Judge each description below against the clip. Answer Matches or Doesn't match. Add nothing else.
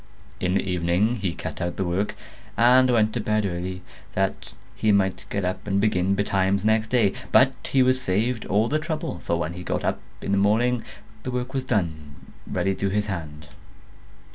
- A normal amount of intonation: Matches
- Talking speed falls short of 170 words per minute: Doesn't match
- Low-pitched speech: Matches